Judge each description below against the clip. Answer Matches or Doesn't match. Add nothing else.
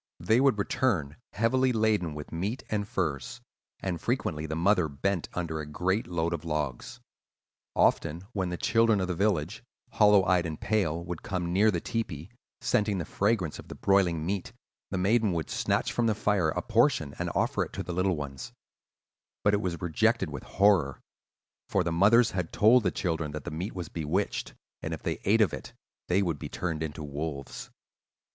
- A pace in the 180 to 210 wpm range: Matches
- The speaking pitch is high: Doesn't match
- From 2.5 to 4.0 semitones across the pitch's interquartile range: Doesn't match